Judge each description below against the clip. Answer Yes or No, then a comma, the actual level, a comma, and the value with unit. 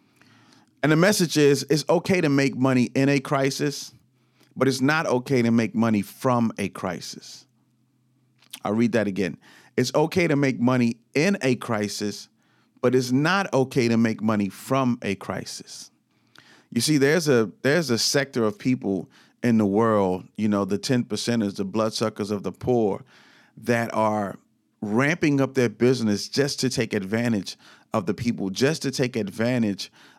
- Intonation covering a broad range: No, average, 3.8 semitones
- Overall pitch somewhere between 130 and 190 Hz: No, low, 120 Hz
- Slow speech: No, average, 165 wpm